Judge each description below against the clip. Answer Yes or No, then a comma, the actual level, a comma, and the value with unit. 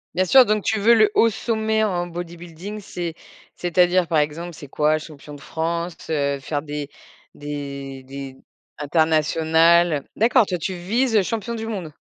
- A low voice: No, medium, 170 Hz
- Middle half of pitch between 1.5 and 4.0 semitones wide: No, average, 5.1 semitones